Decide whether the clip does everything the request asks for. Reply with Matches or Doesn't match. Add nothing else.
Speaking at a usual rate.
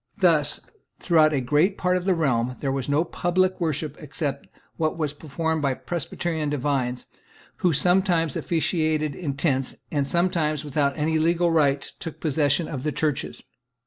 Matches